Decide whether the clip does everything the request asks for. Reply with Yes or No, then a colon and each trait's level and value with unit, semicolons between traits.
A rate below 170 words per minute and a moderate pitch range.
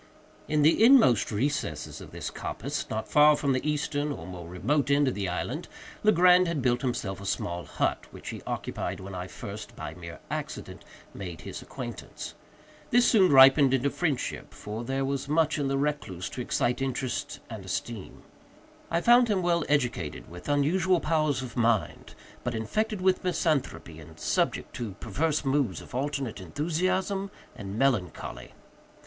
No: average, 160 wpm; wide, 6.8 semitones